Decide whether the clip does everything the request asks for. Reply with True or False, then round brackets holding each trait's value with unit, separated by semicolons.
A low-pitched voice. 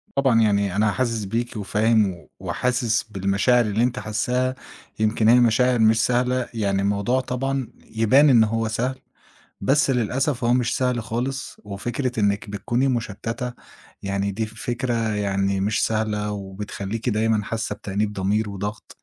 True (110 Hz)